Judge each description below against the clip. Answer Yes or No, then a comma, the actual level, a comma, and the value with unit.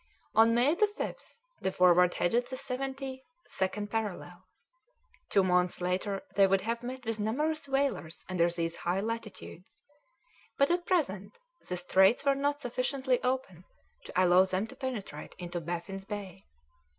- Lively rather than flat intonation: Yes, wide, 6.3 semitones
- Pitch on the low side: No, high, 210 Hz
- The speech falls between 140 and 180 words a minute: Yes, average, 145 wpm